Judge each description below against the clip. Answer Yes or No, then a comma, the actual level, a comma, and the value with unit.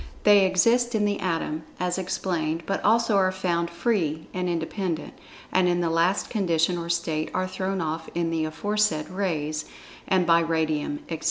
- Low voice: No, medium, 175 Hz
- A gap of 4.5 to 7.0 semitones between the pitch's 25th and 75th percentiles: No, average, 2.8 semitones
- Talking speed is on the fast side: No, average, 170 wpm